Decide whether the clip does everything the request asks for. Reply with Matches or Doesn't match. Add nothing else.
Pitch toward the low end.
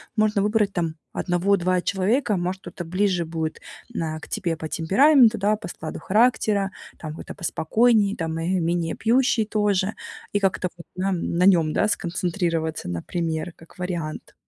Doesn't match